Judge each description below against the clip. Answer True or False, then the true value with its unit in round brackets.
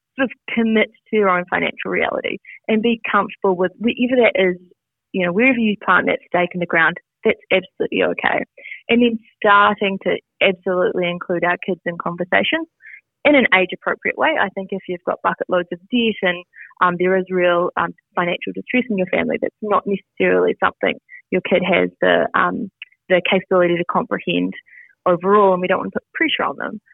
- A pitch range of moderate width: True (3.6 semitones)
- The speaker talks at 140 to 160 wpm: False (190 wpm)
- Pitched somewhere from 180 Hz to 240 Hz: True (190 Hz)